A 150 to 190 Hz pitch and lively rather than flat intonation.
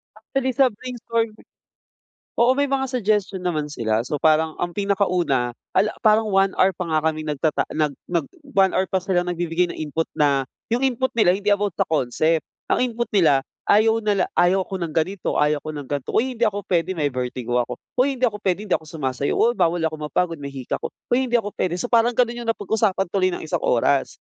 Yes: medium, 185 Hz; wide, 6.1 semitones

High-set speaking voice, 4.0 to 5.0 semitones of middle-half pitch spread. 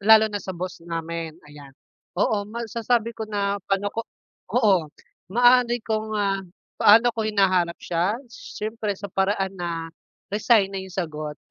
No: high, 200 Hz; average, 3.6 semitones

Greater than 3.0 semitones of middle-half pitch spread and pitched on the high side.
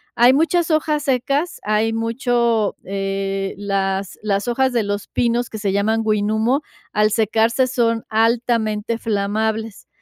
No: average, 2.7 semitones; high, 225 Hz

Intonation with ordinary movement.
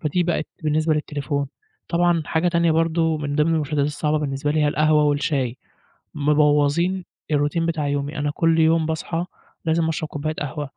No: narrow, 2.0 semitones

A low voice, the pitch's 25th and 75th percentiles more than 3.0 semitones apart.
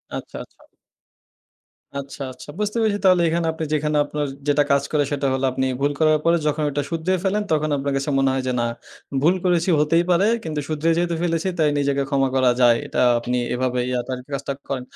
No: medium, 150 Hz; average, 3.4 semitones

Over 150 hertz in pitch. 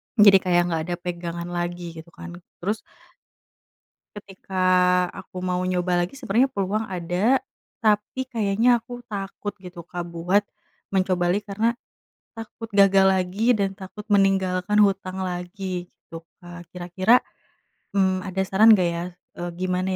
Yes: high, 190 Hz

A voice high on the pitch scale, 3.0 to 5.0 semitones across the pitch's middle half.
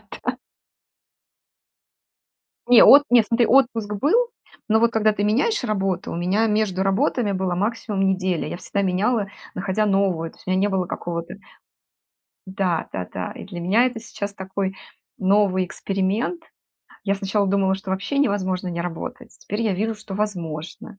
No: high, 200 Hz; narrow, 2.6 semitones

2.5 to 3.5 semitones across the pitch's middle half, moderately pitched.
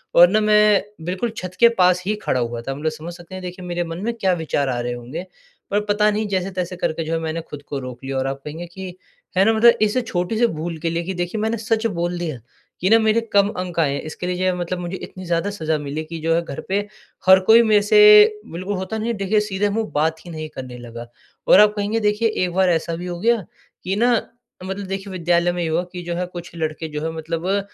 No: average, 4.0 semitones; medium, 180 Hz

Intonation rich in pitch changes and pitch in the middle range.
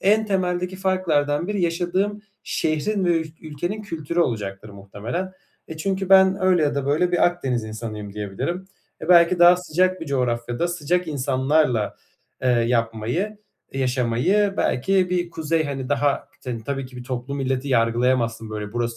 Yes: wide, 6.7 semitones; medium, 145 Hz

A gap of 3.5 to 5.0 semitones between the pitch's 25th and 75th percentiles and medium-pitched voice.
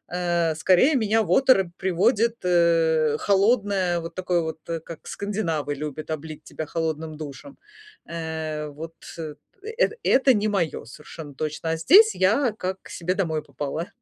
Yes: average, 4.2 semitones; medium, 170 Hz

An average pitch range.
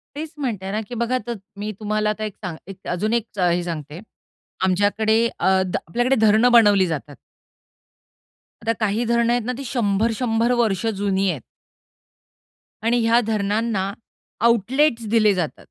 Yes: average, 3.4 semitones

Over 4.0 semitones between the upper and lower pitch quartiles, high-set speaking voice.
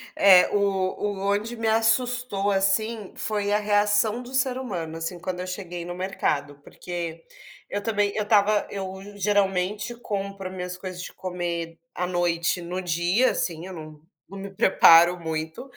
No: average, 2.9 semitones; high, 195 Hz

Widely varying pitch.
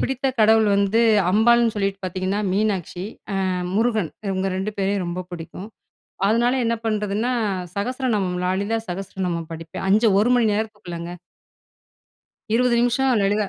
No: average, 3.2 semitones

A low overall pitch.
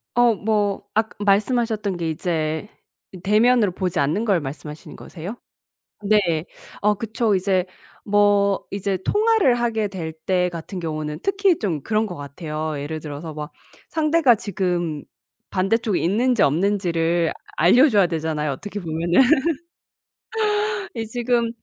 No: high, 190 Hz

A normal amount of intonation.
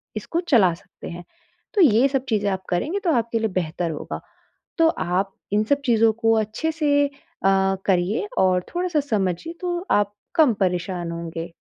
No: wide, 7.6 semitones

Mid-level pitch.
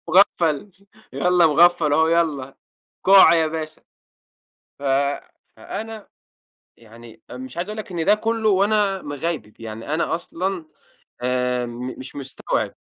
Yes: medium, 165 Hz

